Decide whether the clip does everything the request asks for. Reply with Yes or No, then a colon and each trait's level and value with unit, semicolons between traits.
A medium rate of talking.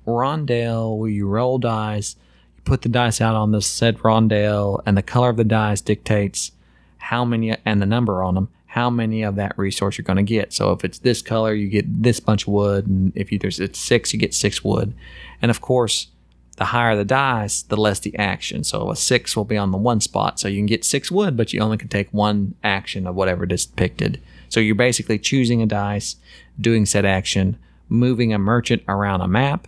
No: fast, 225 wpm